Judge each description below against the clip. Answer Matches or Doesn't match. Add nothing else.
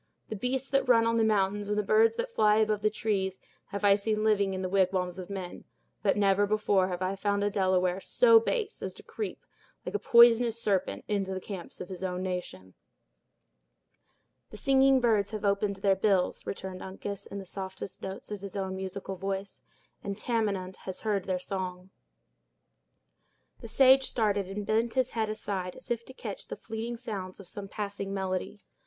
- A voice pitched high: Matches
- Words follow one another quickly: Doesn't match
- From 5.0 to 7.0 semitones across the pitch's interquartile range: Doesn't match